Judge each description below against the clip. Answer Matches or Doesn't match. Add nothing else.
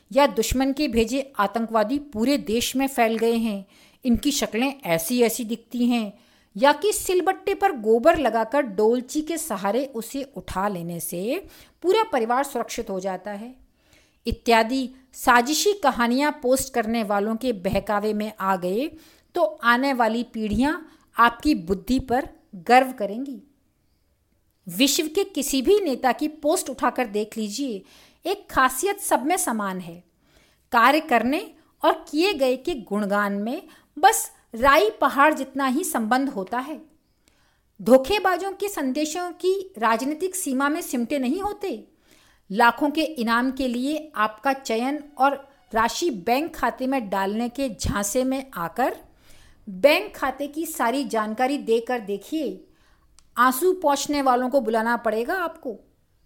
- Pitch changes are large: Doesn't match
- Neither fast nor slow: Matches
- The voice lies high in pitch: Matches